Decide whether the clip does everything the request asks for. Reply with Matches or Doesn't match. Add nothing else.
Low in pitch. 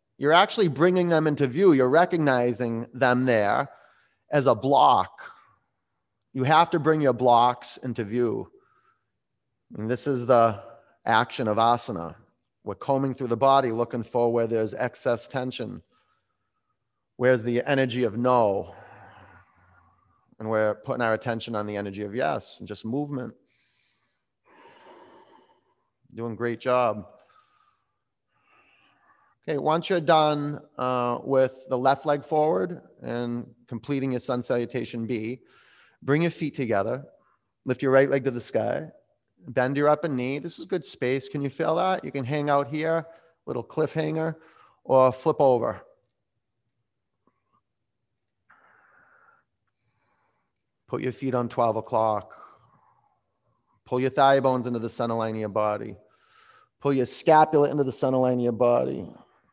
Matches